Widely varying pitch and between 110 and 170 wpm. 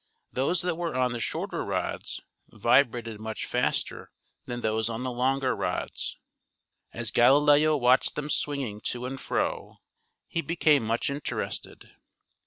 No: average, 3.6 semitones; slow, 135 wpm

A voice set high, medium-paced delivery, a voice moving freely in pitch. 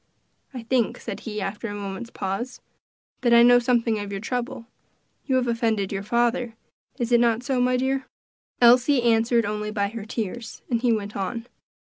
No: high, 230 Hz; average, 185 wpm; narrow, 2.5 semitones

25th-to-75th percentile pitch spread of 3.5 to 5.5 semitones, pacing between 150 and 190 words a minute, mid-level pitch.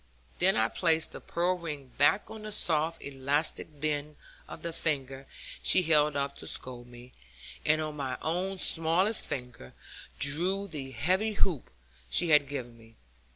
Yes: average, 4.2 semitones; average, 155 wpm; medium, 150 Hz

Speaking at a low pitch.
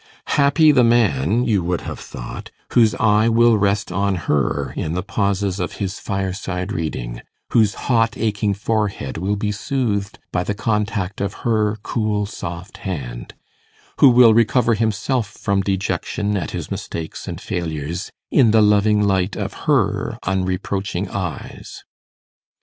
Yes: low, 100 Hz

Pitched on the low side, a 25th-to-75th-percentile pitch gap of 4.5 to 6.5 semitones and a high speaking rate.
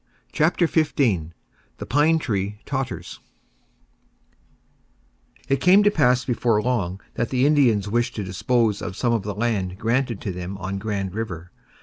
No: low, 115 Hz; average, 5.1 semitones; average, 145 wpm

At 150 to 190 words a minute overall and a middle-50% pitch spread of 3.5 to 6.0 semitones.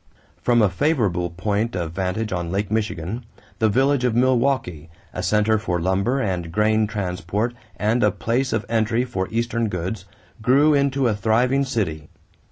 Yes: average, 160 wpm; average, 4.6 semitones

